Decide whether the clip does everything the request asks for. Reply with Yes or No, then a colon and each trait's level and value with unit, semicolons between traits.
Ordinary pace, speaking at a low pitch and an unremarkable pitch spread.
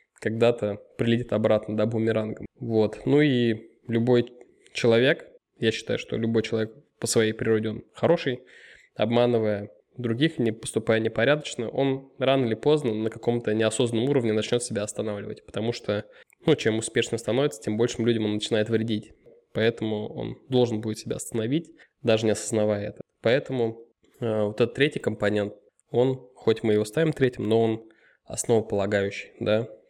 No: average, 150 wpm; low, 115 Hz; narrow, 2.3 semitones